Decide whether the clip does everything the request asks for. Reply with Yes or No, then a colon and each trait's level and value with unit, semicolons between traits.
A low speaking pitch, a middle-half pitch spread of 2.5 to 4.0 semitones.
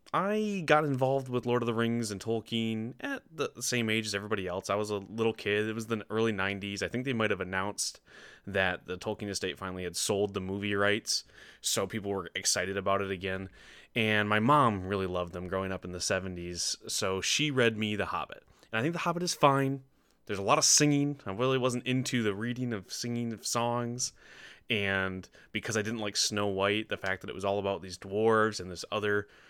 Yes: low, 105 Hz; average, 3.5 semitones